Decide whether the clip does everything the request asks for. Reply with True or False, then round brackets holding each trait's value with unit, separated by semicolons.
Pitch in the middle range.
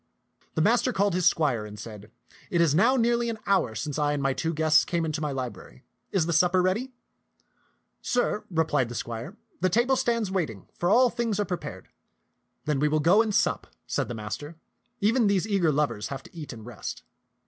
True (170 Hz)